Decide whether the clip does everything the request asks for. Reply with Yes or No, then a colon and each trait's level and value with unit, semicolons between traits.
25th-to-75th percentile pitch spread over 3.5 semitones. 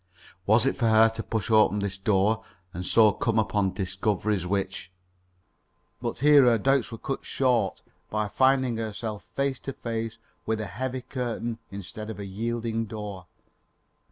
No: average, 2.7 semitones